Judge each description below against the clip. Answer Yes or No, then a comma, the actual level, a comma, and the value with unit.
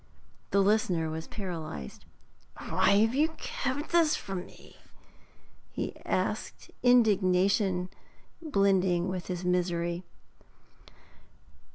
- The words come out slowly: Yes, slow, 90 wpm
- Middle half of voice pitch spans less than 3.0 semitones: No, average, 3.5 semitones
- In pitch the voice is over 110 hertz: Yes, high, 190 Hz